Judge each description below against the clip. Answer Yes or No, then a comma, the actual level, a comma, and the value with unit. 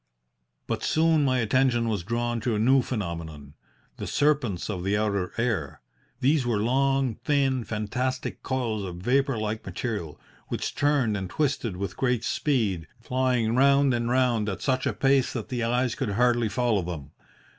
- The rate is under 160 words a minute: No, average, 165 wpm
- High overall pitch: No, low, 120 Hz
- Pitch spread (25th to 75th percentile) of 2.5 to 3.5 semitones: No, average, 4.0 semitones